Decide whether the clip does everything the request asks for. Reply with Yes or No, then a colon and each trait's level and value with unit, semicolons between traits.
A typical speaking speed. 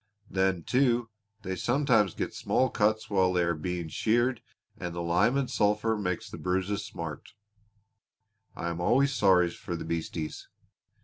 Yes: average, 150 wpm